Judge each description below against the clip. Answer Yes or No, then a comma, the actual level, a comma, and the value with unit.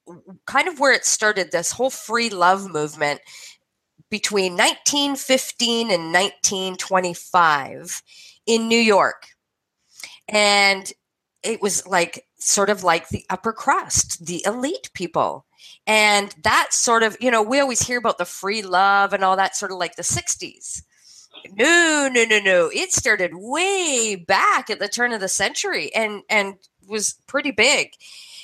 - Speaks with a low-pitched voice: No, high, 205 Hz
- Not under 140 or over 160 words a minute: Yes, average, 150 wpm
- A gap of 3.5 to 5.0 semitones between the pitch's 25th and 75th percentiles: Yes, average, 4.1 semitones